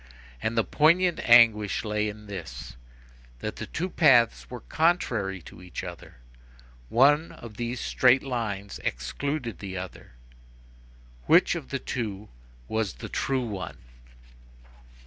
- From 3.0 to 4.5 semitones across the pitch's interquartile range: No, average, 4.9 semitones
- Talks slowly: Yes, slow, 125 wpm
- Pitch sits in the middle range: No, low, 110 Hz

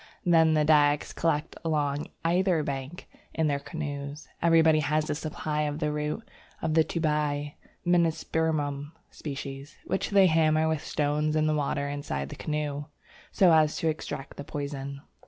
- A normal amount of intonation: No, narrow, 1.7 semitones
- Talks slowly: No, average, 155 wpm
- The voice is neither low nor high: Yes, medium, 150 Hz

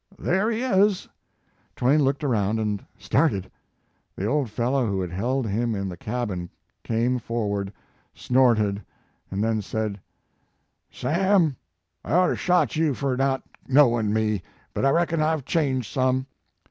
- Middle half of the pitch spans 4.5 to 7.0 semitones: Yes, wide, 5.5 semitones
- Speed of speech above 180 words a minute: No, average, 145 wpm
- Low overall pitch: Yes, low, 125 Hz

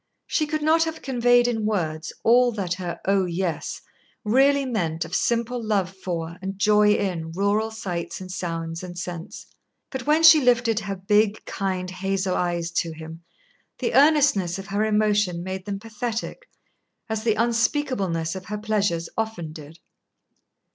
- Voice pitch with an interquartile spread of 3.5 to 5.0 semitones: Yes, average, 4.7 semitones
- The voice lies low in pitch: No, high, 200 Hz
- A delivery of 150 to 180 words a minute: Yes, average, 155 wpm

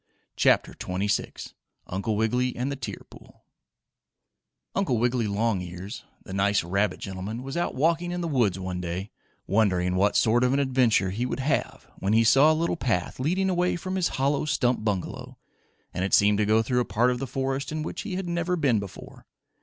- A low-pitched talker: Yes, low, 120 Hz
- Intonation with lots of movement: Yes, wide, 5.9 semitones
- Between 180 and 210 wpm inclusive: Yes, average, 195 wpm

